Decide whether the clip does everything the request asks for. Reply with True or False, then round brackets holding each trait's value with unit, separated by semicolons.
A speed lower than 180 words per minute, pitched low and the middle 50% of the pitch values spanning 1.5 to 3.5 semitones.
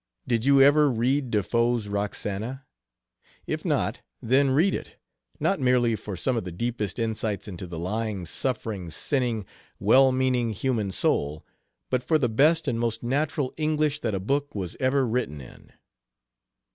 False (160 wpm; 120 Hz; 4.5 semitones)